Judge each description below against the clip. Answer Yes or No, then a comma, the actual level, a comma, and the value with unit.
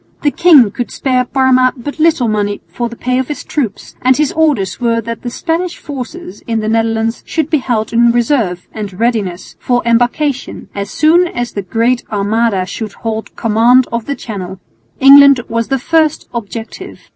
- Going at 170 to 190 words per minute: Yes, average, 180 wpm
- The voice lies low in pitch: No, high, 240 Hz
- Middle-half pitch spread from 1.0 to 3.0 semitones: No, average, 3.7 semitones